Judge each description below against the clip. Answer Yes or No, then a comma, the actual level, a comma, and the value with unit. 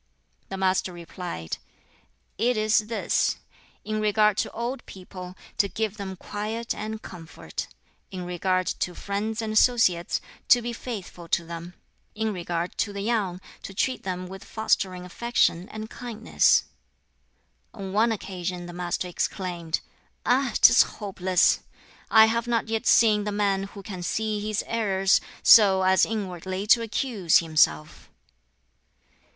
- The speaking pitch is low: No, high, 200 Hz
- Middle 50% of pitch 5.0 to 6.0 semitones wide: No, average, 3.3 semitones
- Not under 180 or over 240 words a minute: No, average, 140 wpm